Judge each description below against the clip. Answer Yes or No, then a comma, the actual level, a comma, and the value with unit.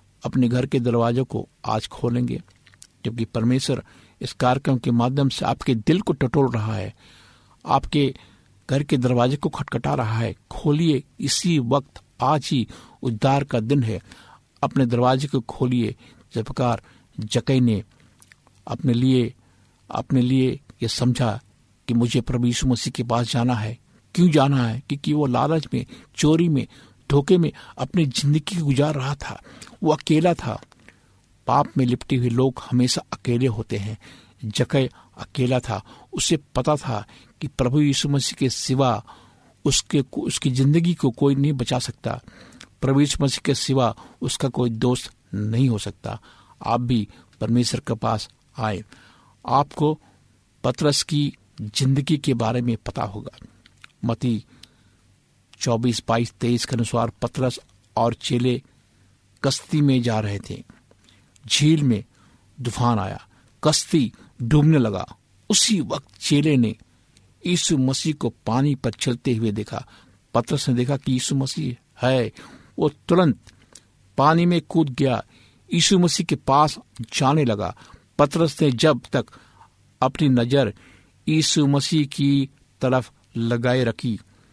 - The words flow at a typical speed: Yes, average, 140 wpm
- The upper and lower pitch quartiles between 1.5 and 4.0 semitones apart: Yes, average, 3.6 semitones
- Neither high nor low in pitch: No, low, 125 Hz